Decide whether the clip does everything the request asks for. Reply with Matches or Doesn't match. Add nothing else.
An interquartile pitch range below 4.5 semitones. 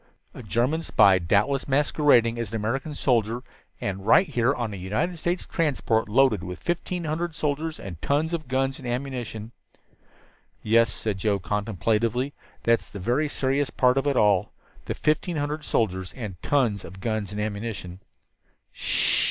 Doesn't match